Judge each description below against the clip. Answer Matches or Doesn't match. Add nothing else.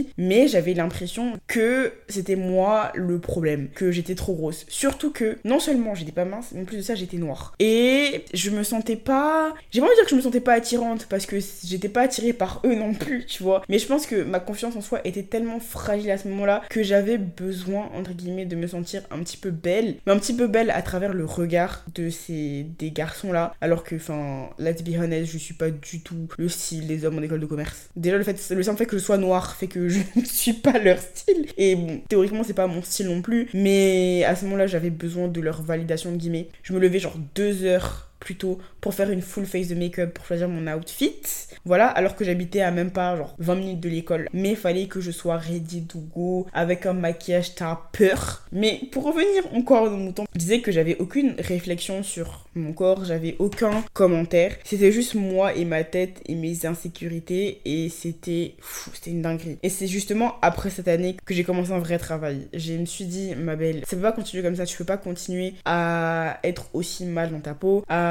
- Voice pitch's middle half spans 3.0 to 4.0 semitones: Matches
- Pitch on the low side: Doesn't match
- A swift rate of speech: Matches